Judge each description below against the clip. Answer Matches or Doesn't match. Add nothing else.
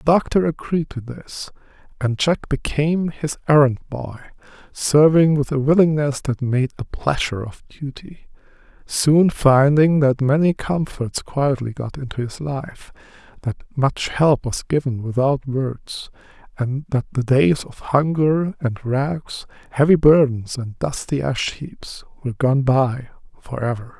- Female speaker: Doesn't match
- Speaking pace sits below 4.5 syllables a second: Matches